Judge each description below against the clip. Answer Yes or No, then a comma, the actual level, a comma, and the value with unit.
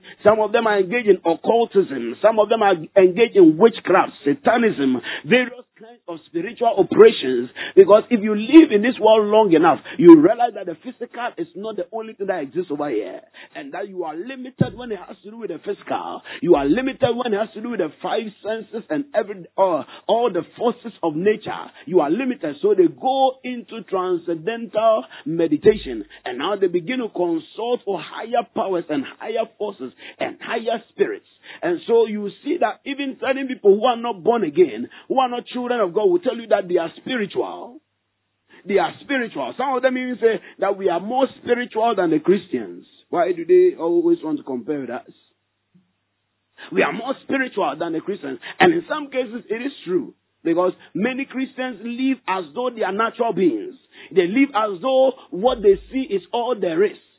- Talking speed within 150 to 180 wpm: No, average, 195 wpm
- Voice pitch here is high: Yes, high, 235 Hz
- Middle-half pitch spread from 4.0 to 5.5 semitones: Yes, average, 5.1 semitones